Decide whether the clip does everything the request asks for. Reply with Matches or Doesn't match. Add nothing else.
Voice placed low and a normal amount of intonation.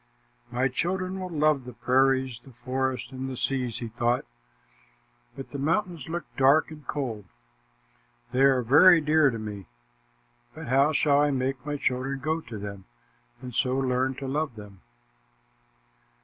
Matches